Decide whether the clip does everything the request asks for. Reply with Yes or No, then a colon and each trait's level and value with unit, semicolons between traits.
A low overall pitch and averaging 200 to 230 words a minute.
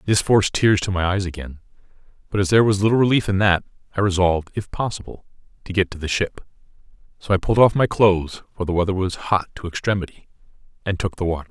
Yes: very low, 95 Hz; fast, 205 wpm